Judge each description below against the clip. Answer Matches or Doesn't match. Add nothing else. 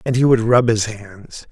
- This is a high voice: Doesn't match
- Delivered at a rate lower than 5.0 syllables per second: Matches